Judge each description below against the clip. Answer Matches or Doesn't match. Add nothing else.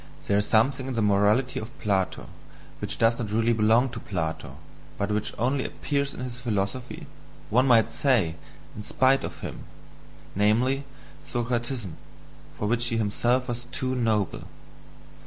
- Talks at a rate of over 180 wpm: Doesn't match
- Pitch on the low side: Matches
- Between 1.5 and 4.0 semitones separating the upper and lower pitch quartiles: Matches